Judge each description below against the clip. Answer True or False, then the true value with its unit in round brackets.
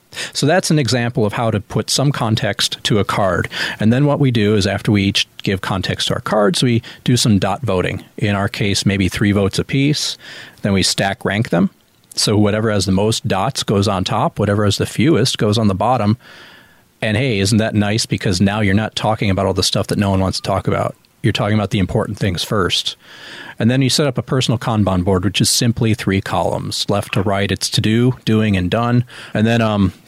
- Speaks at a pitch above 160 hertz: False (110 Hz)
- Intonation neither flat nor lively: True (3.4 semitones)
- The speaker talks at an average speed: False (230 wpm)